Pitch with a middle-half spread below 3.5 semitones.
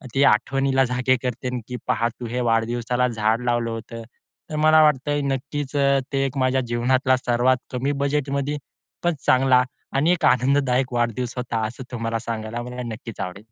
Yes: narrow, 2.5 semitones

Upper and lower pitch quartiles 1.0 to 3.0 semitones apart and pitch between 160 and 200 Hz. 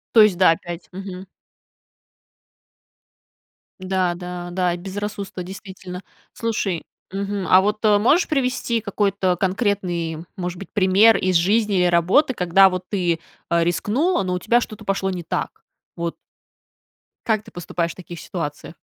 Yes: average, 2.7 semitones; high, 190 Hz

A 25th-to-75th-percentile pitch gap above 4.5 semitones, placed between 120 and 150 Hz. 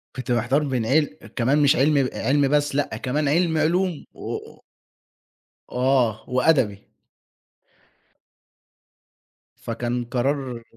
No: average, 3.4 semitones; low, 135 Hz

